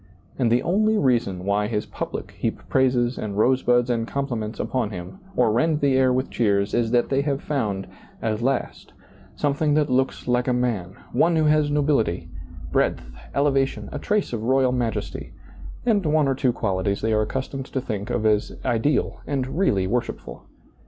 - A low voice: Yes, low, 125 Hz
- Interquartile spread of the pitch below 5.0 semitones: Yes, average, 4.4 semitones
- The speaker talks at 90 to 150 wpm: No, average, 175 wpm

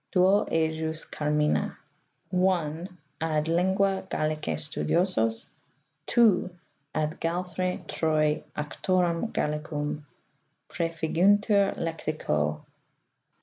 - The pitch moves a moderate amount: Yes, average, 3.3 semitones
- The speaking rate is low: Yes, slow, 75 wpm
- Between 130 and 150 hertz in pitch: No, medium, 165 Hz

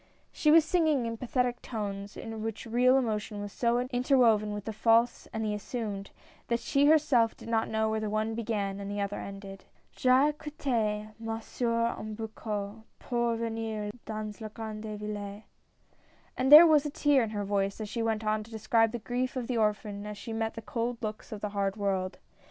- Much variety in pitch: No, narrow, 2.5 semitones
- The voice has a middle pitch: No, high, 220 Hz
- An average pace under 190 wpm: No, average, 200 wpm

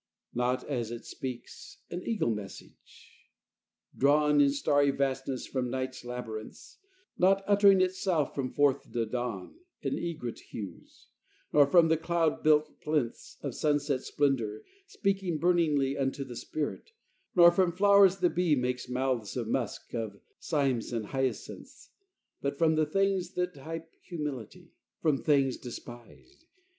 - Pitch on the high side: No, medium, 145 Hz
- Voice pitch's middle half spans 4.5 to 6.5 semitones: Yes, wide, 5.4 semitones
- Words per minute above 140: No, slow, 135 wpm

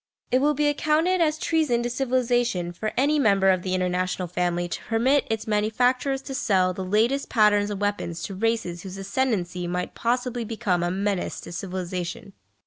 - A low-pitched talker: No, high, 210 Hz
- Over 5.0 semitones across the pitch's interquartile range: Yes, wide, 5.6 semitones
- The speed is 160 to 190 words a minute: Yes, average, 175 wpm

